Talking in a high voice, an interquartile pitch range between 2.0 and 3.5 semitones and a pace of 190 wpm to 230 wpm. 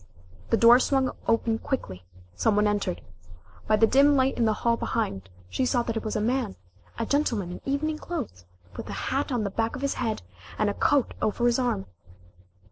No: high, 230 Hz; average, 4.1 semitones; fast, 205 wpm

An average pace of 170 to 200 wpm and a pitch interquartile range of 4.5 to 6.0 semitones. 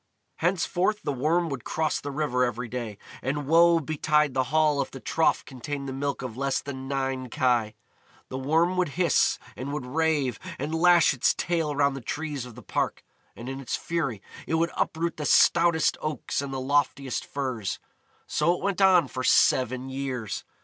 No: average, 185 wpm; average, 3.8 semitones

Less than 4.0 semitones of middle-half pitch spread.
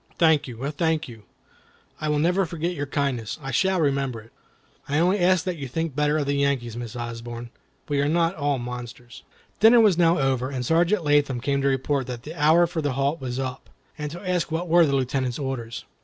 No: average, 4.3 semitones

